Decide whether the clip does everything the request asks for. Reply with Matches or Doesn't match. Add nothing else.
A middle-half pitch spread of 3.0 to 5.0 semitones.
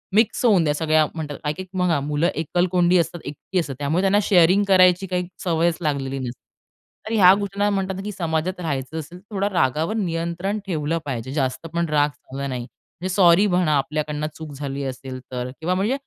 Matches